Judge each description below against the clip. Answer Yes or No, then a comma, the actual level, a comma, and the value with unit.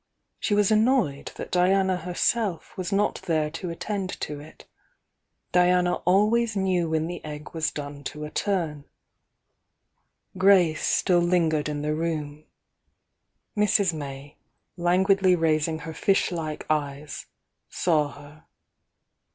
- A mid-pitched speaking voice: Yes, medium, 170 Hz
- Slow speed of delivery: Yes, slow, 125 wpm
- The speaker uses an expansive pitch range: No, average, 3.8 semitones